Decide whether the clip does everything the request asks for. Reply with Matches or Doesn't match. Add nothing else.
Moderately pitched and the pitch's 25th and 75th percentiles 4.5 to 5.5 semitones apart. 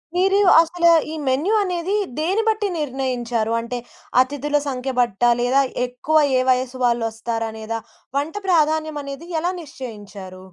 Doesn't match